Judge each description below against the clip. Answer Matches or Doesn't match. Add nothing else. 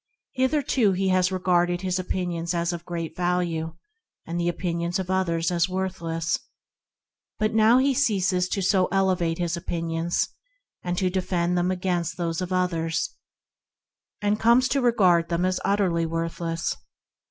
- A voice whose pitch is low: Doesn't match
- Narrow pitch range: Matches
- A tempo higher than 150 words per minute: Doesn't match